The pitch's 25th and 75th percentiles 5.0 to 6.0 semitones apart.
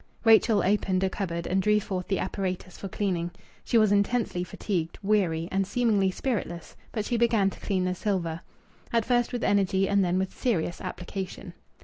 No: narrow, 2.6 semitones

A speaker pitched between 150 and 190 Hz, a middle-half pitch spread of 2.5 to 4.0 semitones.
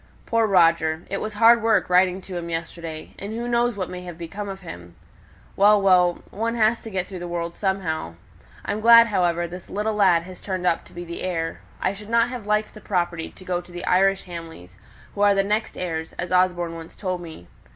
Yes: medium, 185 Hz; average, 3.4 semitones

